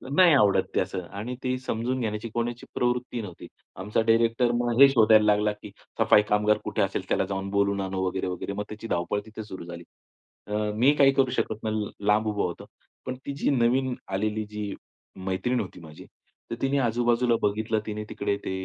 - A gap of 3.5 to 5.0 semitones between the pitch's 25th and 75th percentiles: No, average, 3.0 semitones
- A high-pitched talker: No, low, 110 Hz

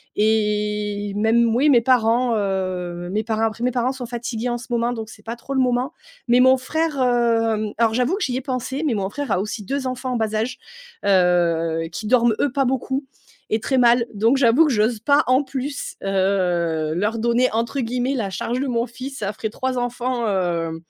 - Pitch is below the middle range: No, high, 235 Hz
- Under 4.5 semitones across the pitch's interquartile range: Yes, average, 3.4 semitones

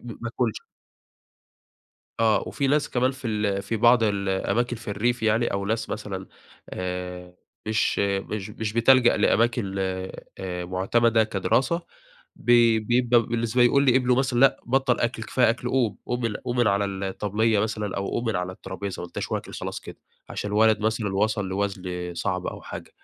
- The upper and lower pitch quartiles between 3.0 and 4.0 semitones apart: Yes, average, 3.4 semitones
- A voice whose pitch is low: Yes, low, 110 Hz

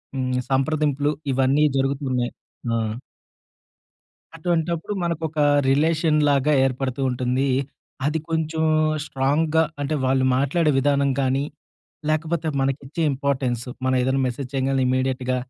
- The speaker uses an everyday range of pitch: Yes, average, 3.0 semitones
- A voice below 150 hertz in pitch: Yes, medium, 140 Hz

